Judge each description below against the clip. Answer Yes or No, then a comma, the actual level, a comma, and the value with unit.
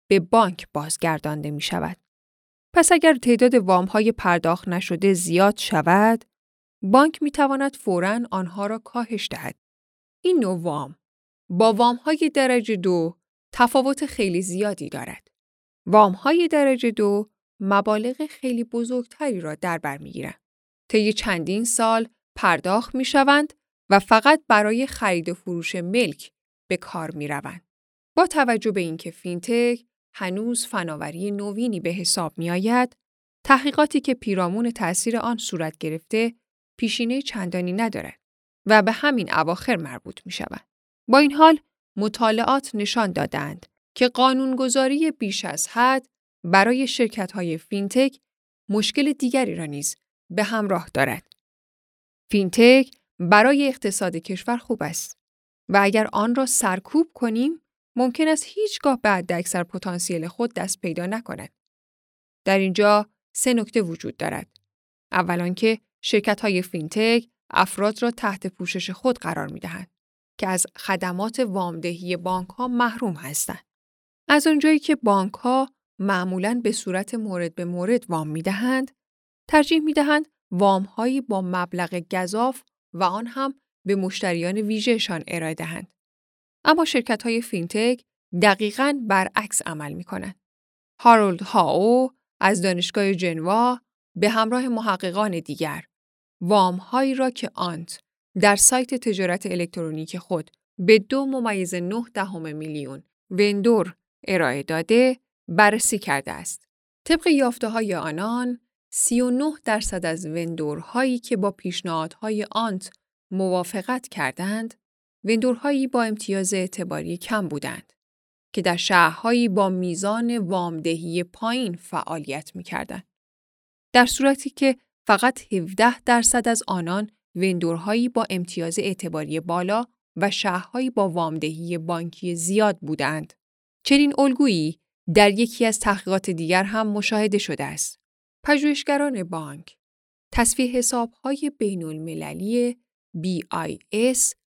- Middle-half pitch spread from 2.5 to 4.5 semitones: No, average, 5.3 semitones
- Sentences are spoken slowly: No, average, 125 wpm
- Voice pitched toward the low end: No, high, 210 Hz